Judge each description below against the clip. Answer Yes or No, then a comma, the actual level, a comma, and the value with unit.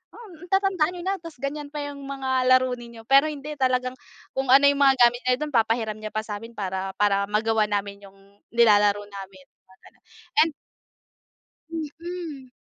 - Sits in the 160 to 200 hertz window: No, very high, 250 Hz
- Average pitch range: No, wide, 5.8 semitones